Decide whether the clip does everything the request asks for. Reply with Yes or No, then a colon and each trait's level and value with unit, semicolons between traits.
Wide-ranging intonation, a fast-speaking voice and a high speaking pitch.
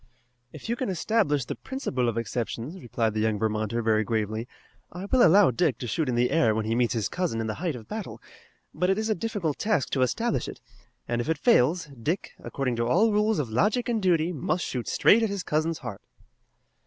No: wide, 8.9 semitones; fast, 220 wpm; medium, 145 Hz